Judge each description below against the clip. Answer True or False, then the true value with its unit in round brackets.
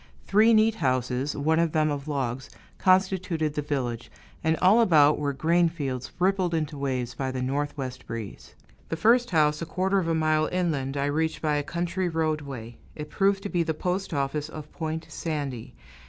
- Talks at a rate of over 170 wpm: True (180 wpm)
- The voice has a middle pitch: True (155 Hz)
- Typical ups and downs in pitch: True (3.9 semitones)